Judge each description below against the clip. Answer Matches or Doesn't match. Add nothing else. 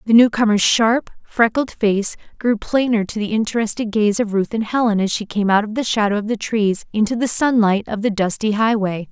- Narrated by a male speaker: Doesn't match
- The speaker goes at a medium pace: Doesn't match